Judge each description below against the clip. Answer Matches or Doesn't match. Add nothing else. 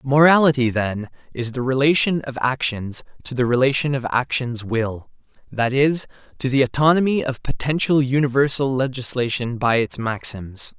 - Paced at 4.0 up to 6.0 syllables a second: Matches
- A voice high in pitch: Doesn't match